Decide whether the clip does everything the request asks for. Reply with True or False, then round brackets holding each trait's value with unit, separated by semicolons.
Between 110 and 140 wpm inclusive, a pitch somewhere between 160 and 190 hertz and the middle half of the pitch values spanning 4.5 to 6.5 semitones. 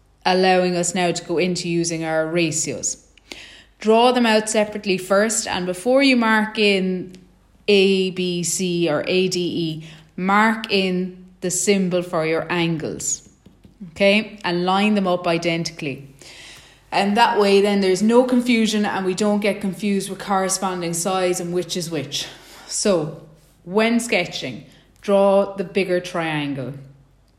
False (135 wpm; 185 Hz; 3.1 semitones)